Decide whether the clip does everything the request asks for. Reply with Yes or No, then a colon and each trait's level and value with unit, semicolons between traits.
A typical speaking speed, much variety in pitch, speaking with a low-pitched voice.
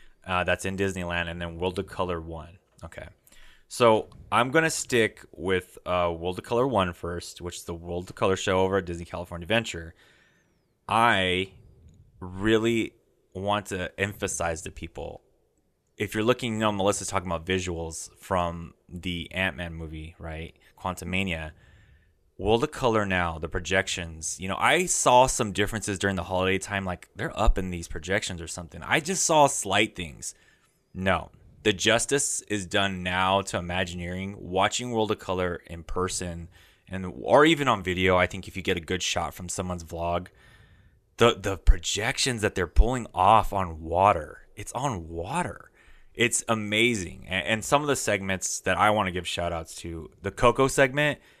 No: average, 175 wpm; average, 3.3 semitones; very low, 95 Hz